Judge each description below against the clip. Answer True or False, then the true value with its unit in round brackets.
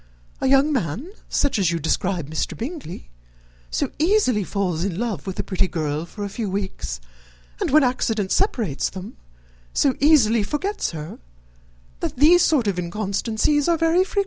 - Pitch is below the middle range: False (215 Hz)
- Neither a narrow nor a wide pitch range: False (8.3 semitones)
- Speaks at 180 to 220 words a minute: False (165 wpm)